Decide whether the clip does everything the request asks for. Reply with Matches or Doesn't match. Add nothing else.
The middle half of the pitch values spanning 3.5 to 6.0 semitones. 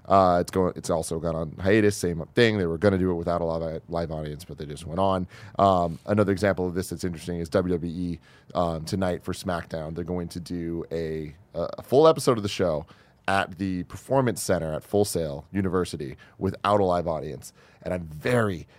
Doesn't match